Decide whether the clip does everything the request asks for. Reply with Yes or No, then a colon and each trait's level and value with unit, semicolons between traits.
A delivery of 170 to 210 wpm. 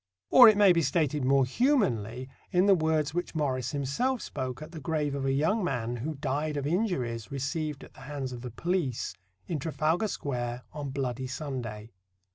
Yes: average, 185 wpm